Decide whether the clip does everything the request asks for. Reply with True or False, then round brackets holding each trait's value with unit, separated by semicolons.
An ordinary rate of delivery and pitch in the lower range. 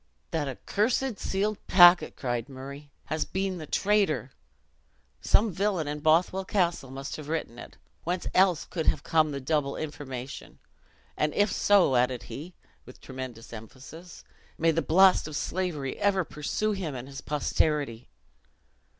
False (145 wpm; 155 Hz)